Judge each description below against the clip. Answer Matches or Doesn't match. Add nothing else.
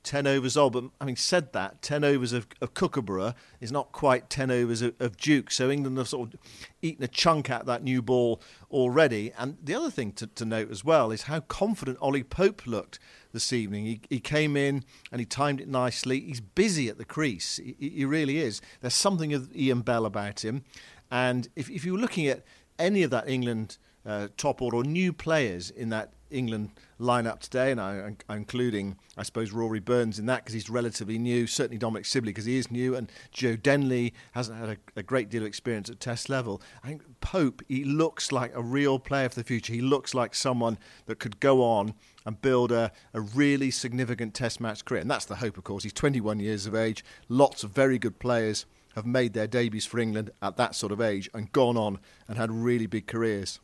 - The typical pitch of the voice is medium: Doesn't match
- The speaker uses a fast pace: Matches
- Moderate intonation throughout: Matches